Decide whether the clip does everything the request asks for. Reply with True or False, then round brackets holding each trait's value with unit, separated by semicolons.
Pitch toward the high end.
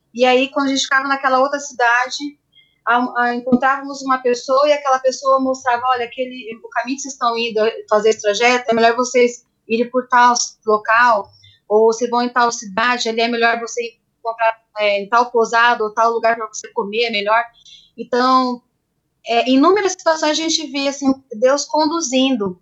True (240 Hz)